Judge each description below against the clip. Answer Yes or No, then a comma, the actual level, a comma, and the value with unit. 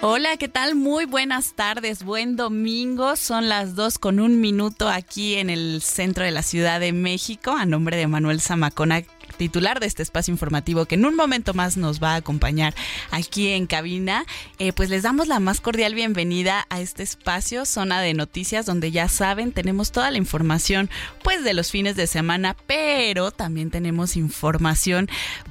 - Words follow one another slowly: No, average, 180 wpm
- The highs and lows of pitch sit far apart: No, average, 4.7 semitones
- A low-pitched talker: No, high, 190 Hz